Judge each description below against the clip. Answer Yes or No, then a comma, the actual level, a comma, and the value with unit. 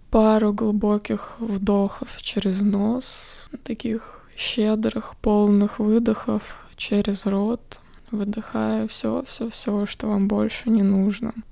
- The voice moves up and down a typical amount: No, narrow, 1.7 semitones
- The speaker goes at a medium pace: No, slow, 105 wpm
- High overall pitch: Yes, high, 210 Hz